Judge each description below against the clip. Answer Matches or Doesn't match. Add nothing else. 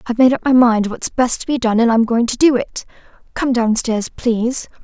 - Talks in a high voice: Matches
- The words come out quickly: Matches